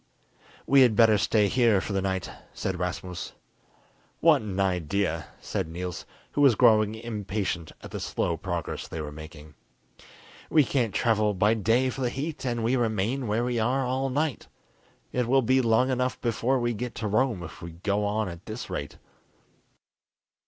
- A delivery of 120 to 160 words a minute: No, average, 175 wpm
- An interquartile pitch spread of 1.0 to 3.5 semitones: No, average, 4.7 semitones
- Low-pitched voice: Yes, low, 110 Hz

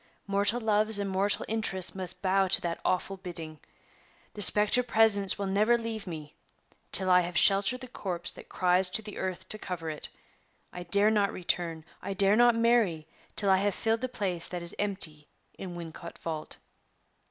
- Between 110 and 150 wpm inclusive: No, average, 180 wpm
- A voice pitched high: Yes, high, 195 Hz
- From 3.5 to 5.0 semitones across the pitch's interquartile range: No, average, 3.1 semitones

